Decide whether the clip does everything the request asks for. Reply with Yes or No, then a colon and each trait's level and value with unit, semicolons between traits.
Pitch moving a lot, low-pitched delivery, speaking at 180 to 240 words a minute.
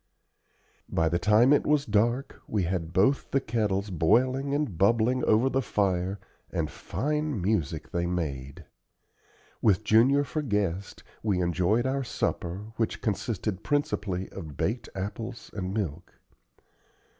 No: wide, 5.8 semitones; low, 105 Hz; slow, 135 wpm